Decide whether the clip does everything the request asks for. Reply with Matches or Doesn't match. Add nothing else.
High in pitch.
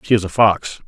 Doesn't match